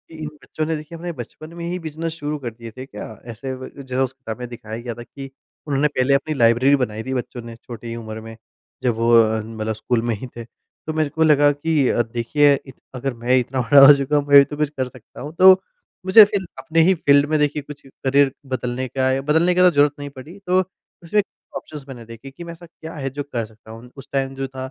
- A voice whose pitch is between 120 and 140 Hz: Yes, low, 135 Hz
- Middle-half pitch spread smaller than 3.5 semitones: No, average, 4.1 semitones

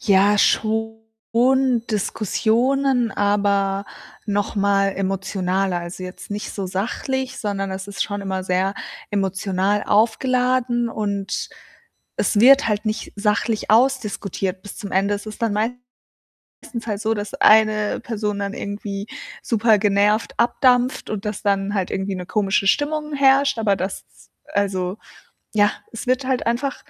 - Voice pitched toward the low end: No, high, 210 Hz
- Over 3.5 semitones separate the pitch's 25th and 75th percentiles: No, average, 2.9 semitones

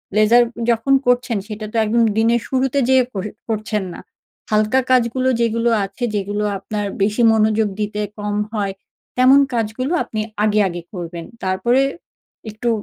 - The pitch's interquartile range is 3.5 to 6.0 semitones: No, narrow, 2.5 semitones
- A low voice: No, high, 220 Hz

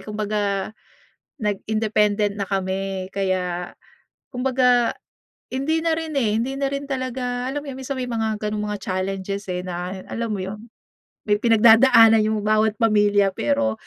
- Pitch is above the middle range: Yes, high, 215 Hz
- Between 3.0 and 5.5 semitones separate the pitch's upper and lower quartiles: Yes, average, 3.9 semitones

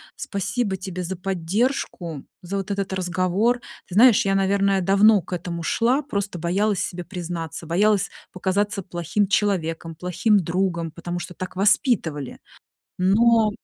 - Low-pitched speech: No, high, 190 Hz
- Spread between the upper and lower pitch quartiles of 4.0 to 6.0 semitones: No, average, 2.8 semitones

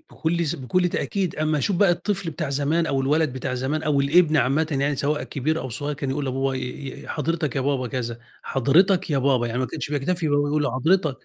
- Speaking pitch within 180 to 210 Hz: No, medium, 145 Hz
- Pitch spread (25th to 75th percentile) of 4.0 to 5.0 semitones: No, average, 3.2 semitones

